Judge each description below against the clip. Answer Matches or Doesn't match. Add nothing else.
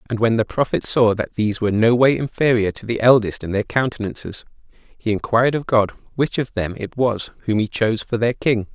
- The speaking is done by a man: Matches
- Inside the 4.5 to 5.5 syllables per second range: Doesn't match